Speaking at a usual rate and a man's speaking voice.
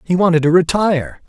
Yes: average, 190 wpm; male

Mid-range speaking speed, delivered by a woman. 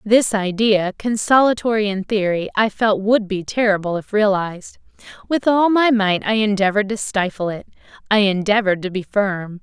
Yes: average, 155 wpm; female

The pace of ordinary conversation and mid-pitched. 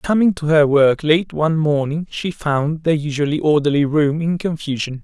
Yes: average, 180 wpm; medium, 150 Hz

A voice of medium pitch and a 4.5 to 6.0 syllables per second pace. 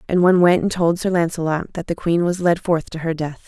Yes: medium, 170 Hz; 5.8 syllables/s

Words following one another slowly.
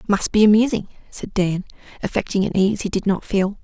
No: average, 200 wpm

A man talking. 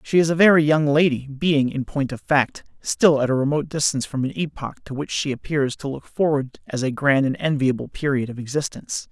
Yes: male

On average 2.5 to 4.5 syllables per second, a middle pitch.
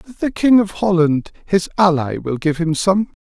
Yes: 4.1 syllables/s; medium, 180 Hz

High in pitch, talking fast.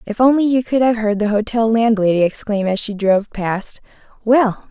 No: high, 220 Hz; average, 190 wpm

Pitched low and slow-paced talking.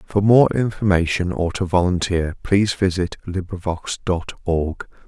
Yes: very low, 90 Hz; slow, 130 wpm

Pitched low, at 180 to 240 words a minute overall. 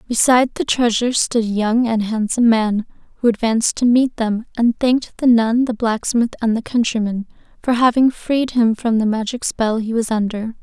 No: high, 230 Hz; average, 190 wpm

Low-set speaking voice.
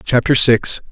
Yes: low, 120 Hz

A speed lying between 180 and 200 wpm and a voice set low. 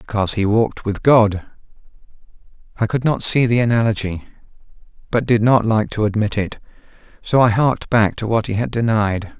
No: average, 170 wpm; low, 110 Hz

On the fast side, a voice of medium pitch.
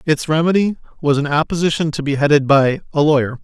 No: average, 190 wpm; medium, 150 Hz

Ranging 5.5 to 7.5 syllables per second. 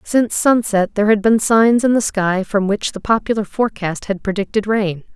No: 5.2 syllables/s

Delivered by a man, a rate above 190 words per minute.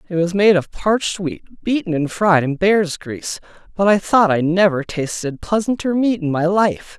Yes: male; average, 200 wpm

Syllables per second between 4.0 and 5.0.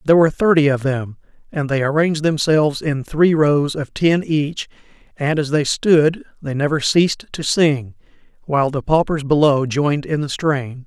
Yes: 4.9 syllables/s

